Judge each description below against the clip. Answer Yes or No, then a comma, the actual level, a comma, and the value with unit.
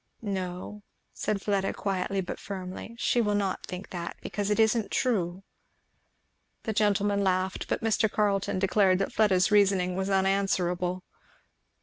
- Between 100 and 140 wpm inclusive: Yes, slow, 135 wpm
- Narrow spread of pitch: Yes, narrow, 2.0 semitones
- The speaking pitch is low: No, high, 195 Hz